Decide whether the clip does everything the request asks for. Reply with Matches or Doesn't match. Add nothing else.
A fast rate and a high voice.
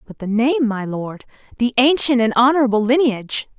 Doesn't match